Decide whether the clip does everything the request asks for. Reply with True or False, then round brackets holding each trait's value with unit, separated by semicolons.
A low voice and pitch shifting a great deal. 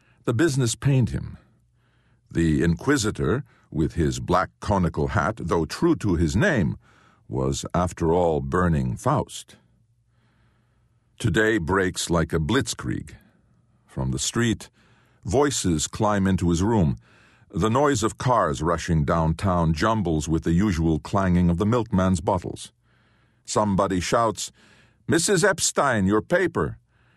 True (100 Hz; 5.7 semitones)